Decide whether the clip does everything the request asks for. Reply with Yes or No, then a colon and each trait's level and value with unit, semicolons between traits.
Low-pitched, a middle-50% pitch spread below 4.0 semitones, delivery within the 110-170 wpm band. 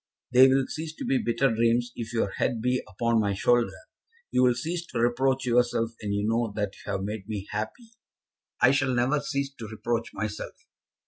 No: low, 120 Hz; average, 3.2 semitones; average, 195 wpm